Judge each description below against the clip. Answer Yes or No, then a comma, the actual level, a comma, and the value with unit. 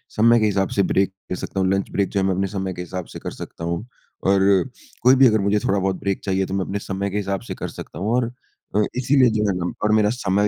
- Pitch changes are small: Yes, narrow, 2.0 semitones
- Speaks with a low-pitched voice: Yes, low, 100 Hz